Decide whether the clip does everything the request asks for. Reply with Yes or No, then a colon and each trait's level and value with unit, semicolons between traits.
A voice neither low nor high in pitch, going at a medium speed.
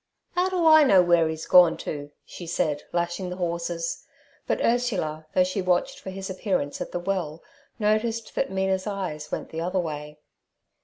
Yes: medium, 180 Hz; average, 175 wpm